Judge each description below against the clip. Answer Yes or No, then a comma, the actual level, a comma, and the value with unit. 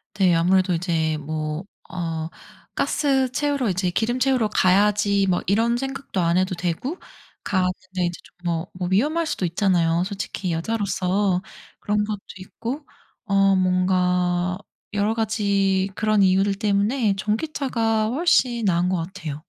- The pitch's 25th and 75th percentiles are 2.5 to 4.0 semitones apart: Yes, average, 3.6 semitones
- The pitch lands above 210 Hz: No, high, 195 Hz